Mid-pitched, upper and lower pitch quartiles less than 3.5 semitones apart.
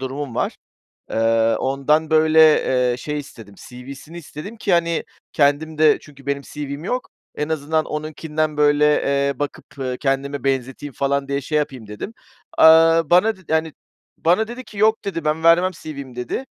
Yes: medium, 150 Hz; average, 2.8 semitones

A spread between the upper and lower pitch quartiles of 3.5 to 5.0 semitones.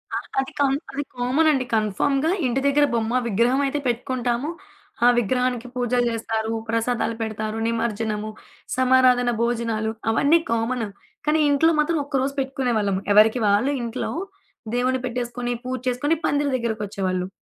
No: average, 2.9 semitones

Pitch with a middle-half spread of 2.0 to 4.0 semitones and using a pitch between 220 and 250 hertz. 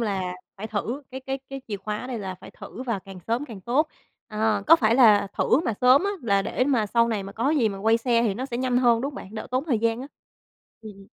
Yes: average, 3.7 semitones; high, 230 Hz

